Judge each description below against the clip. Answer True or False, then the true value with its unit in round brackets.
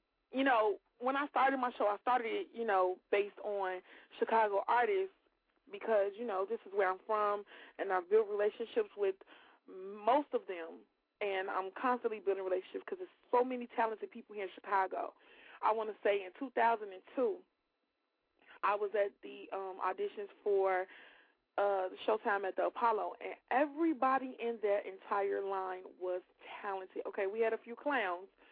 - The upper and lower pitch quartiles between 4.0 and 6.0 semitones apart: True (5.0 semitones)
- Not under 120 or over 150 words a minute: False (165 wpm)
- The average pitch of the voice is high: True (215 Hz)